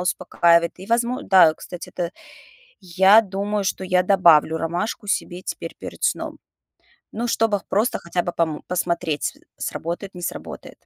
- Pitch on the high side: No, medium, 180 Hz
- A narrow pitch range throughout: No, average, 3.1 semitones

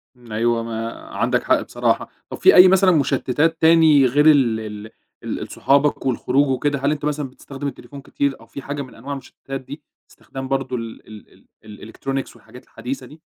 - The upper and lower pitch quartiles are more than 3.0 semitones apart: Yes, average, 3.4 semitones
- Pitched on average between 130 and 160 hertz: Yes, low, 135 Hz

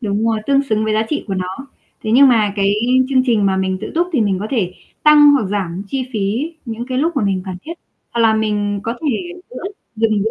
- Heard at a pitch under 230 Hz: Yes, high, 220 Hz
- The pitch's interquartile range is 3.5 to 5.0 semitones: Yes, average, 4.6 semitones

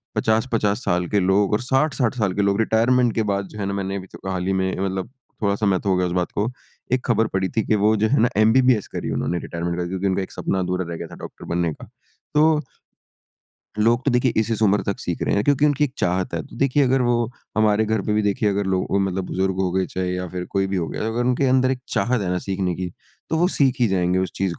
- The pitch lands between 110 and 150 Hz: No, low, 100 Hz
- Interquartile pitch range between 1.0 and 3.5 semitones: No, average, 4.2 semitones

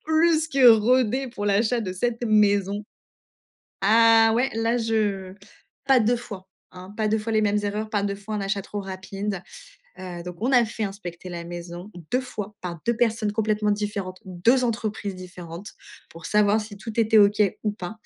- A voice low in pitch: No, high, 210 Hz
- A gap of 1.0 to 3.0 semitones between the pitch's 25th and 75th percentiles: Yes, average, 2.7 semitones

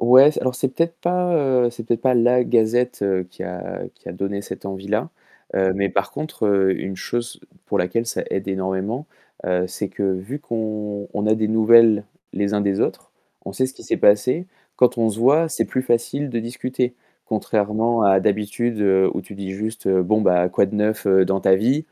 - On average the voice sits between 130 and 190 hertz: No, low, 110 Hz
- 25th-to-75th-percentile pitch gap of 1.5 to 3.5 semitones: No, average, 3.9 semitones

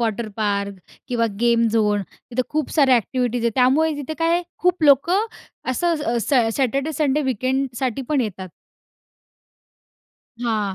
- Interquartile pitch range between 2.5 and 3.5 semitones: No, average, 4.2 semitones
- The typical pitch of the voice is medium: No, very high, 255 Hz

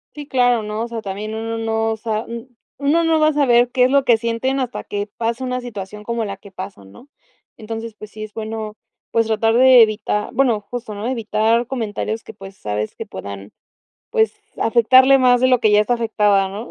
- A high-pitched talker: Yes, high, 225 Hz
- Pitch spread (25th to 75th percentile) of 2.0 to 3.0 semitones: Yes, average, 2.7 semitones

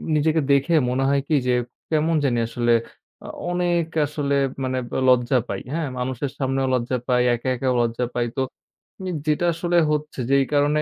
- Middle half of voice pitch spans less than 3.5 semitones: Yes, average, 3.1 semitones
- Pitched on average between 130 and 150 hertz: Yes, medium, 140 Hz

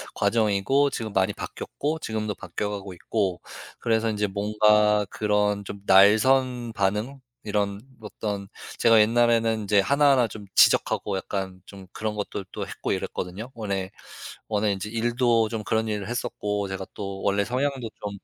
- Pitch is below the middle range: Yes, low, 105 Hz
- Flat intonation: Yes, narrow, 2.3 semitones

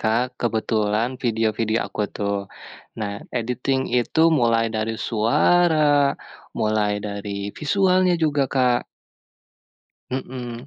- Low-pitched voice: Yes, low, 120 Hz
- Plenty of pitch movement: No, average, 3.9 semitones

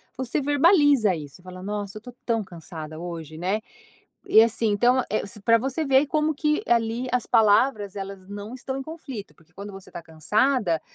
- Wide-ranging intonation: Yes, wide, 5.7 semitones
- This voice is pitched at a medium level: No, high, 215 Hz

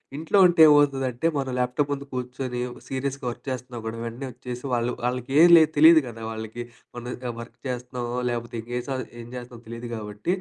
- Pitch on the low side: Yes, low, 125 Hz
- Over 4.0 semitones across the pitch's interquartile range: No, narrow, 2.5 semitones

